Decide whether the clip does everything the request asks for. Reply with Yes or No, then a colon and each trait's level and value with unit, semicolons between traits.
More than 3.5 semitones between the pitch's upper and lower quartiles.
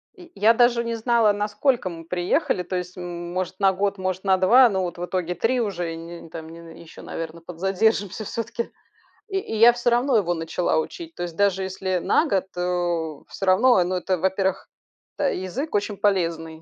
Yes: average, 4.2 semitones